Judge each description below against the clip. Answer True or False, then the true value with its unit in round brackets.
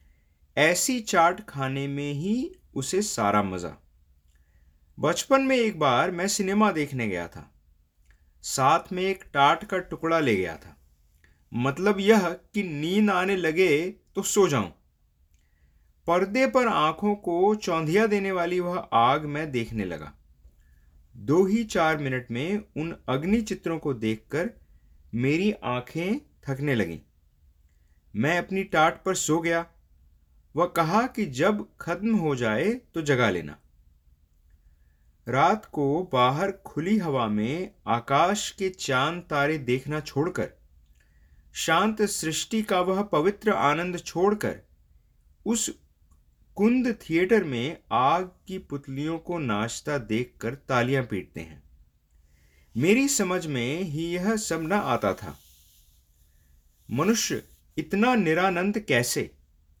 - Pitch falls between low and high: True (145 Hz)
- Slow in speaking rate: True (120 wpm)